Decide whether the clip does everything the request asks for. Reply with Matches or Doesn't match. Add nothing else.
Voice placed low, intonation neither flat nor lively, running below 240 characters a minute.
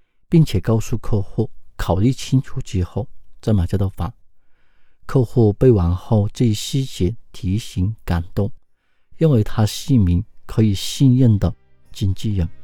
Matches